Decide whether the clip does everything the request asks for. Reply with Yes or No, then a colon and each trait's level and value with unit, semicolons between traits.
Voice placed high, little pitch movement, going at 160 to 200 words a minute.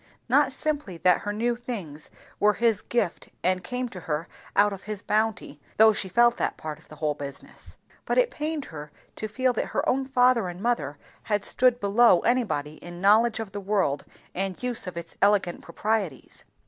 No: high, 205 Hz; wide, 5.5 semitones; average, 190 wpm